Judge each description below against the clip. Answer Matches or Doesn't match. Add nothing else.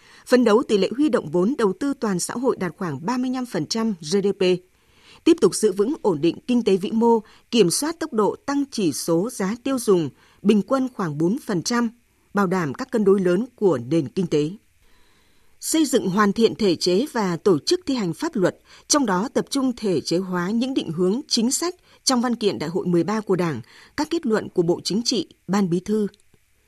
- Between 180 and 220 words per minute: Matches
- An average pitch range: Doesn't match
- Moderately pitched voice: Doesn't match